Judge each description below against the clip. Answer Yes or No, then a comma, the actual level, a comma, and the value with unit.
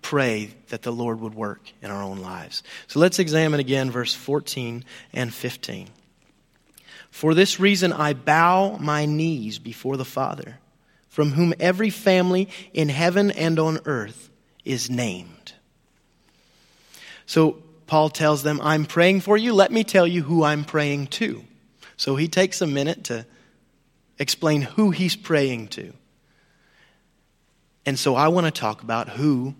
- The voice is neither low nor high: Yes, medium, 150 Hz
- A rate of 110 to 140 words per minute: No, average, 150 wpm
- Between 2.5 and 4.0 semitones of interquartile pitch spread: No, wide, 5.5 semitones